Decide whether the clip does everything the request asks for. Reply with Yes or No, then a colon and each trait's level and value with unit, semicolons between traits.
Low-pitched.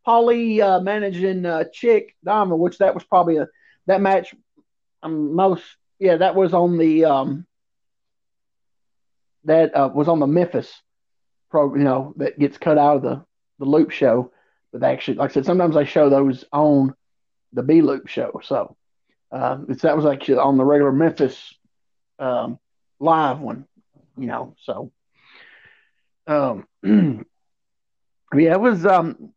No: medium, 160 Hz